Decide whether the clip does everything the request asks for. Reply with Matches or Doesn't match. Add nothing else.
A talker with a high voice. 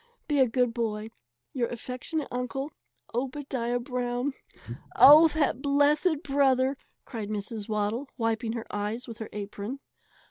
Matches